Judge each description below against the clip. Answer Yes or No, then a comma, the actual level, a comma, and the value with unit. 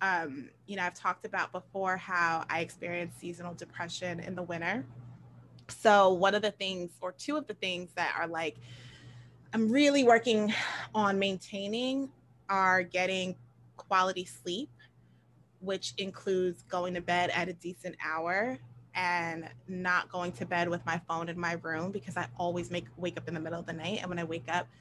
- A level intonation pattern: Yes, narrow, 2.2 semitones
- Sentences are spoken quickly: No, average, 180 wpm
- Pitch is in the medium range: Yes, medium, 175 Hz